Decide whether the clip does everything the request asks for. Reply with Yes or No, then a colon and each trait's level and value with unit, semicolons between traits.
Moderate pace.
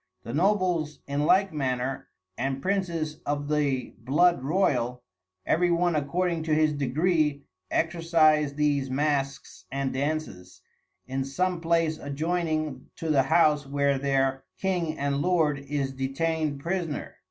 No: slow, 130 wpm